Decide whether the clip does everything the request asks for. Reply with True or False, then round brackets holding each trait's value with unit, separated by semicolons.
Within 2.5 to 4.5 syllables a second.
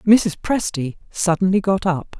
True (4.0 syllables/s)